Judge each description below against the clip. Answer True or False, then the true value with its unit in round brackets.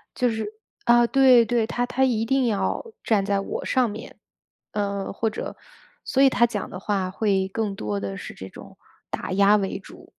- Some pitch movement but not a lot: True (3.6 semitones)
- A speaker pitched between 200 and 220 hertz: True (215 Hz)